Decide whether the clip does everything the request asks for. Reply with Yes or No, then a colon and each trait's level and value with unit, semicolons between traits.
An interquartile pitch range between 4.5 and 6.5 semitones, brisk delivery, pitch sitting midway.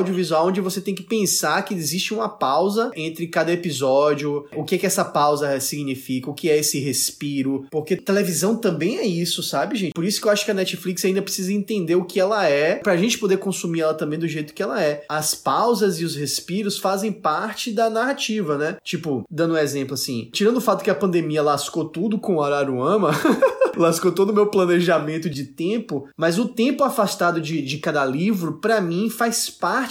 Yes: average, 5.0 semitones; fast, 205 wpm; medium, 175 Hz